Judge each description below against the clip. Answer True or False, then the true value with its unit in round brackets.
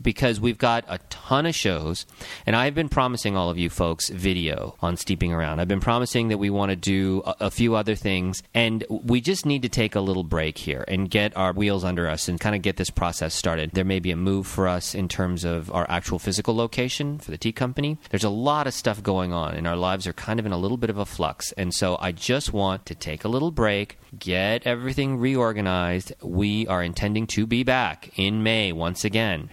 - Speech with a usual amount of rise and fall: True (4.4 semitones)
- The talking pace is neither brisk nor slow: False (235 wpm)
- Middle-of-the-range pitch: False (100 Hz)